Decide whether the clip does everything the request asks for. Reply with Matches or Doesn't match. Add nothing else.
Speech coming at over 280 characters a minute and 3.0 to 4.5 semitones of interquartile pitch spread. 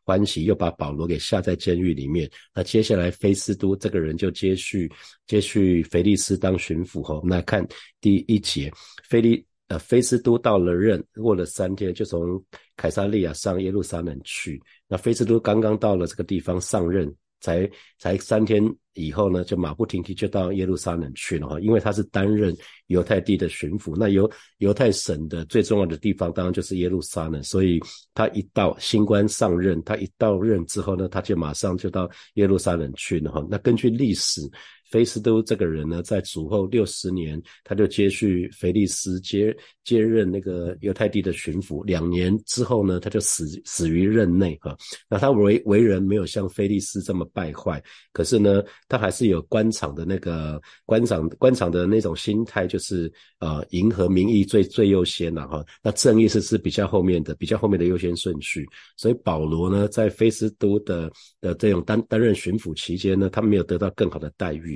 Matches